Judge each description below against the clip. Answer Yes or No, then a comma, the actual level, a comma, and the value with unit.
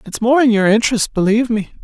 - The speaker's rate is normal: No, fast, 230 wpm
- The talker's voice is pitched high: Yes, high, 225 Hz